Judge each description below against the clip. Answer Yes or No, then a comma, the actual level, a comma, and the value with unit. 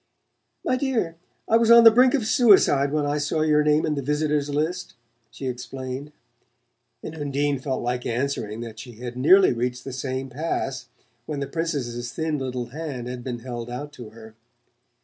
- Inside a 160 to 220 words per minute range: Yes, average, 180 wpm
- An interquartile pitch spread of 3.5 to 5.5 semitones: Yes, average, 3.9 semitones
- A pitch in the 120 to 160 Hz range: Yes, medium, 140 Hz